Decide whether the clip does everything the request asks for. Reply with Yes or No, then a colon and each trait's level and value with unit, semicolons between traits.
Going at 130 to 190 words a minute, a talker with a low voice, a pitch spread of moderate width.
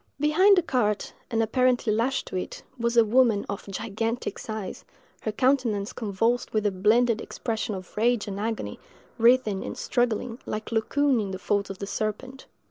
No: average, 170 wpm; high, 225 Hz; average, 3.0 semitones